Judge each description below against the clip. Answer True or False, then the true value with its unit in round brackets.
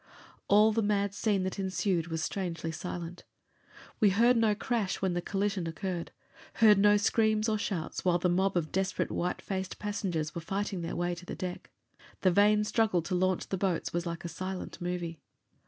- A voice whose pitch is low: False (190 Hz)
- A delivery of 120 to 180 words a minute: False (190 wpm)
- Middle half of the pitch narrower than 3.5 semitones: True (3.0 semitones)